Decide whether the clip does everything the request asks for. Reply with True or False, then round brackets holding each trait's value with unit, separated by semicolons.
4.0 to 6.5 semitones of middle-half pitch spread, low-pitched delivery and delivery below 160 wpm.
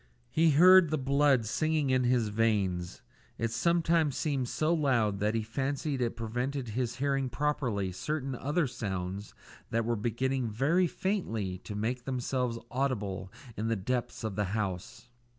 True (4.6 semitones; 125 Hz; 150 wpm)